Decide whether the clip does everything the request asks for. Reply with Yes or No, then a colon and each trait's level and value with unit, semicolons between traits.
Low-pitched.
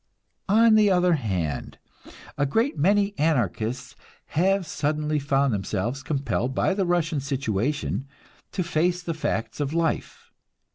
No: medium, 150 Hz